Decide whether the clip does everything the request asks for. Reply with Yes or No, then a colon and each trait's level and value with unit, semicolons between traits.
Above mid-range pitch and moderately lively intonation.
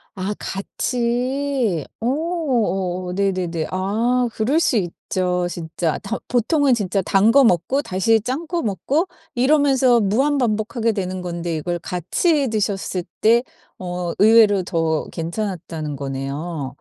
No: high, 200 Hz; wide, 5.8 semitones